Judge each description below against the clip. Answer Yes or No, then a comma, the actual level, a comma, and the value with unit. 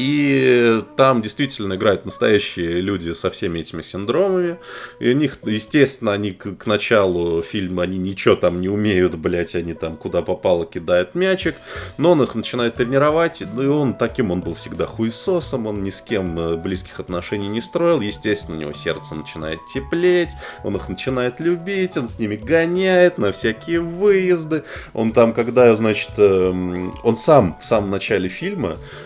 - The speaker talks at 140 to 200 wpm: Yes, fast, 160 wpm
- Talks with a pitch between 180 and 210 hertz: No, low, 110 Hz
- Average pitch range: No, wide, 7.6 semitones